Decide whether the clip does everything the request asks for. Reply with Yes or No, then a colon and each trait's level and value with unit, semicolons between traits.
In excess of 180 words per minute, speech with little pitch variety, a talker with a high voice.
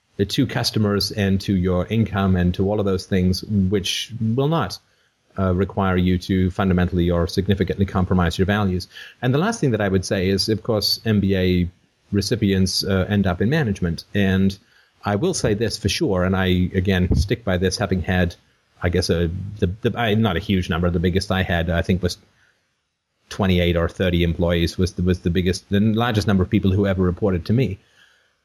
No: average, 200 wpm; narrow, 2.3 semitones; very low, 95 Hz